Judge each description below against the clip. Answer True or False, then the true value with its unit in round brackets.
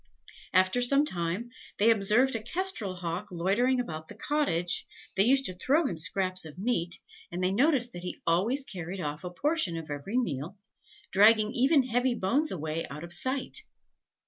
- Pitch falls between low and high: False (200 Hz)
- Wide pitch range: True (6.5 semitones)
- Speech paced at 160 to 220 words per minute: True (170 wpm)